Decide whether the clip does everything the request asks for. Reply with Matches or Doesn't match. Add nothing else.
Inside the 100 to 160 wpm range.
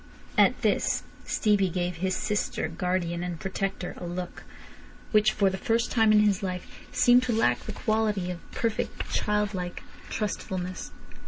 Matches